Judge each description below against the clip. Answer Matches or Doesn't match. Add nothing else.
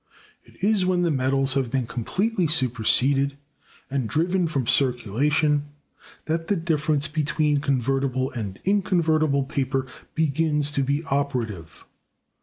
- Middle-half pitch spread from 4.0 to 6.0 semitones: Doesn't match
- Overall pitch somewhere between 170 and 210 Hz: Doesn't match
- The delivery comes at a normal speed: Doesn't match